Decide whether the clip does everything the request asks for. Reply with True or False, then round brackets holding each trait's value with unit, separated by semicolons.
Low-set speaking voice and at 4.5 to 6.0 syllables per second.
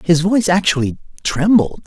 False (180 Hz; 5.4 syllables/s)